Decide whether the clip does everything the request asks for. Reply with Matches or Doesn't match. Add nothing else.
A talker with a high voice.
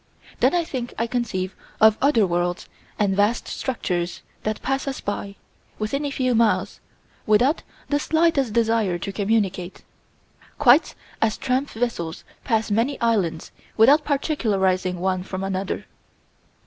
Matches